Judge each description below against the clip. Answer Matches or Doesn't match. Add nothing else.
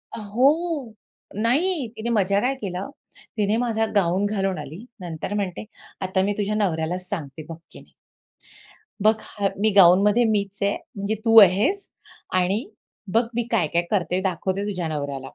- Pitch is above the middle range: Matches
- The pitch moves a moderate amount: Matches